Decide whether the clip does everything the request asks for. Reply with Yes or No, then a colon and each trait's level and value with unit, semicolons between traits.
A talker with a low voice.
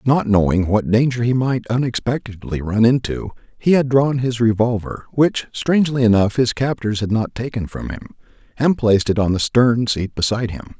Yes: low, 115 Hz